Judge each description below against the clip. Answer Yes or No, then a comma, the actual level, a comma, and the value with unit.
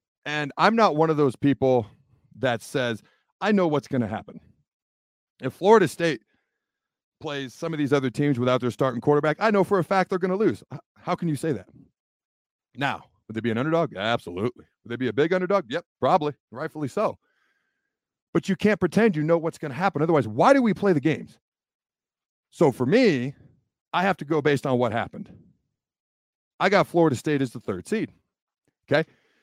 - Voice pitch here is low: No, medium, 150 Hz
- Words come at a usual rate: Yes, average, 195 wpm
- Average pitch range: No, wide, 5.9 semitones